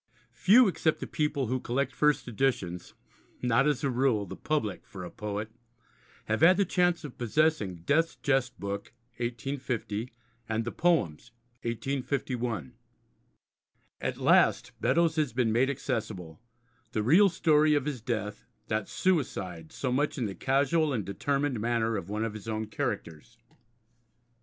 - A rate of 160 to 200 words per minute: No, average, 145 wpm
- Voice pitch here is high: No, low, 125 Hz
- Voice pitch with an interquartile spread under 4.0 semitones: No, average, 5.3 semitones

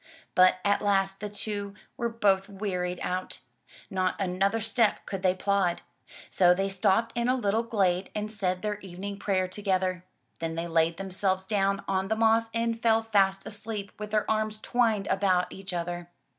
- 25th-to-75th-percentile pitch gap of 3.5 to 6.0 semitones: No, narrow, 2.5 semitones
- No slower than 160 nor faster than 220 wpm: Yes, average, 170 wpm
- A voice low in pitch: No, high, 195 Hz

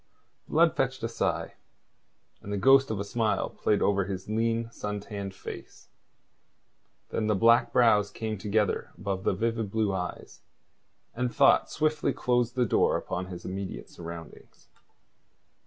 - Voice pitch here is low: Yes, low, 110 Hz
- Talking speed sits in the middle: Yes, average, 145 wpm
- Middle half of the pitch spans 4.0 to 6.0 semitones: No, average, 3.1 semitones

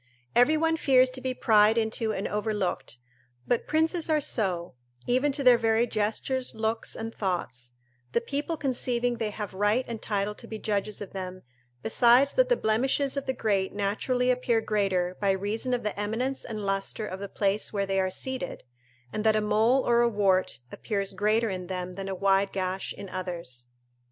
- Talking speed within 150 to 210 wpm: Yes, average, 185 wpm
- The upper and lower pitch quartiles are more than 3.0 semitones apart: Yes, average, 4.1 semitones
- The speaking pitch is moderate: No, high, 215 Hz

